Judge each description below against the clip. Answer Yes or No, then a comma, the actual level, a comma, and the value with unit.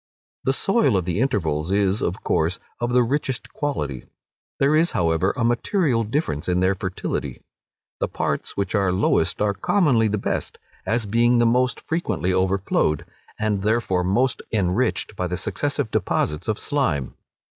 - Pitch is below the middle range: Yes, low, 105 Hz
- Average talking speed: Yes, average, 155 wpm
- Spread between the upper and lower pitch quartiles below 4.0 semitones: No, average, 5.3 semitones